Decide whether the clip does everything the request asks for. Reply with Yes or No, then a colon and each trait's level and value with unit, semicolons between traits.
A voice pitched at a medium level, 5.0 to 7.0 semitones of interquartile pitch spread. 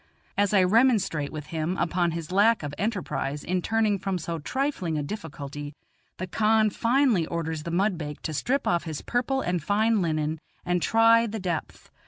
Yes: medium, 180 Hz; wide, 5.6 semitones